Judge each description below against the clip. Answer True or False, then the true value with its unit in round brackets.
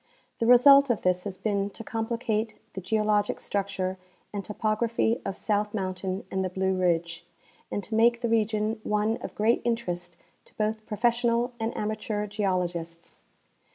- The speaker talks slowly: False (155 wpm)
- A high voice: True (210 Hz)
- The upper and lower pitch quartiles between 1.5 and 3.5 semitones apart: True (3.1 semitones)